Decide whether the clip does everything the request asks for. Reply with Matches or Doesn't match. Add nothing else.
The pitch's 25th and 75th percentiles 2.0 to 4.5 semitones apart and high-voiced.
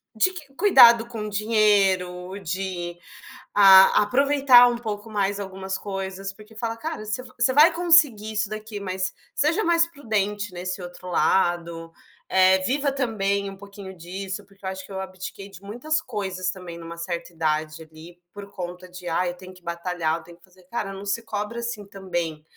Matches